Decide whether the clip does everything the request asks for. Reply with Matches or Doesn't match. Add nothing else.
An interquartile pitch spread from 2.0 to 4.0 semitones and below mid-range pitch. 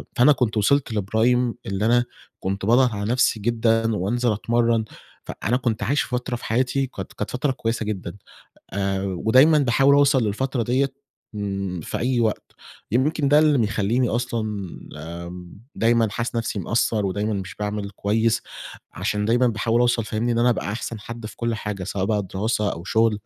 Matches